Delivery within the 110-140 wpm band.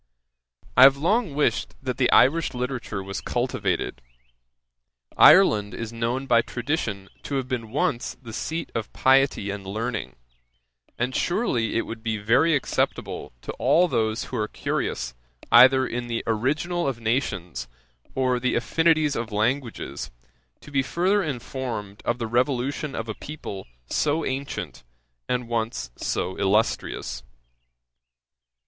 Yes: slow, 135 wpm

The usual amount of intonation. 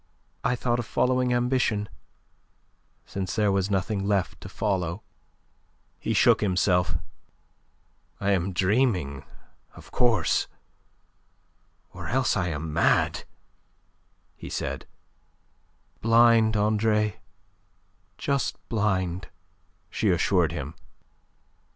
Yes: average, 4.0 semitones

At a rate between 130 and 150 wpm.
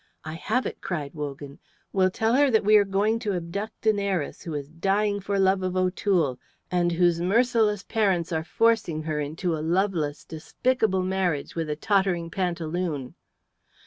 No: average, 170 wpm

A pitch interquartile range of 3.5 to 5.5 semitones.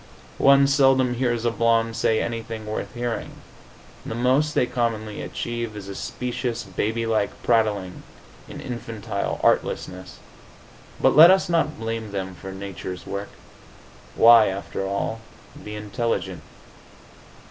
No: average, 3.1 semitones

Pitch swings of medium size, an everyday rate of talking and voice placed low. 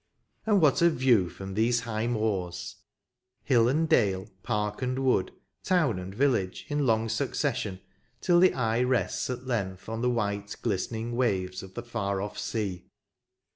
Yes: average, 4.3 semitones; average, 170 wpm; low, 115 Hz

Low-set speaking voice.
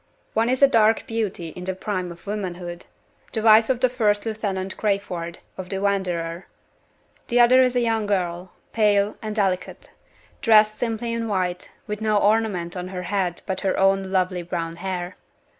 No: high, 200 Hz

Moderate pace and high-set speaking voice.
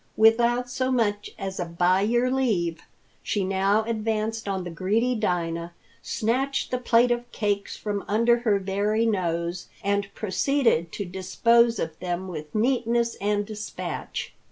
Yes: average, 145 wpm; high, 210 Hz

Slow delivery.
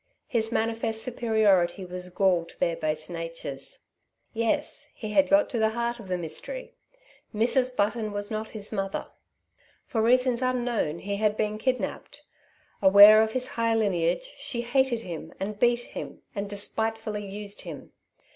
No: average, 155 wpm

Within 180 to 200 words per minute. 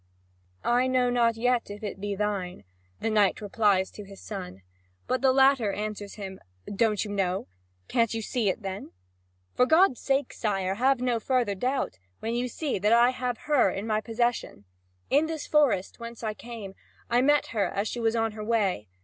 Yes: average, 190 wpm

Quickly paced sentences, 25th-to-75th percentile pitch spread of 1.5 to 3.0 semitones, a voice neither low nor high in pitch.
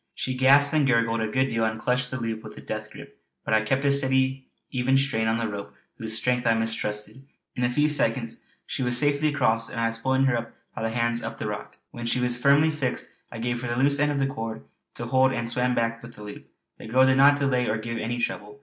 No: fast, 260 wpm; average, 2.7 semitones; low, 125 Hz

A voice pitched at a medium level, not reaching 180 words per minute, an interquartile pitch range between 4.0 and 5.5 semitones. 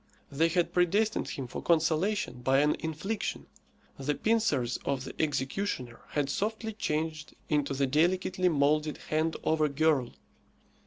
Yes: medium, 155 Hz; average, 140 wpm; average, 4.3 semitones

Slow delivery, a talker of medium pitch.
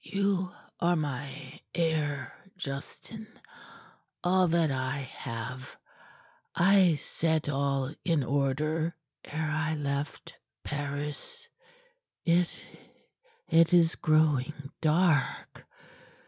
Yes: slow, 85 wpm; medium, 155 Hz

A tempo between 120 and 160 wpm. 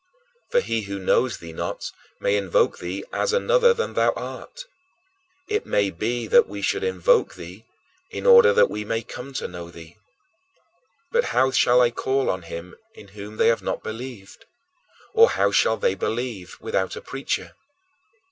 No: average, 170 wpm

